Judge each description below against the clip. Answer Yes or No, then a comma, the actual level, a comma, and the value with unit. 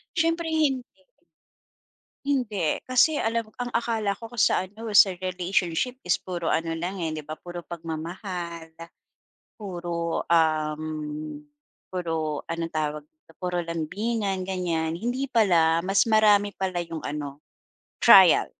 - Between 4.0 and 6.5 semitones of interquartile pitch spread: Yes, average, 4.7 semitones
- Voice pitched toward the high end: No, medium, 175 Hz